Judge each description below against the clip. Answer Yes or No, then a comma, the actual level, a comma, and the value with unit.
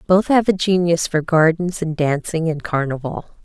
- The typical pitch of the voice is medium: Yes, medium, 165 Hz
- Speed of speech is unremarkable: Yes, average, 175 wpm